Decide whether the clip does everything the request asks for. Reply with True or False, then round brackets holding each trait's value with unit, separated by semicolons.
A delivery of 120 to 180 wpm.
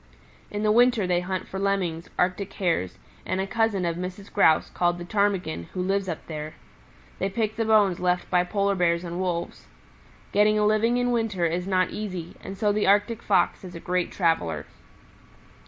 False (190 wpm)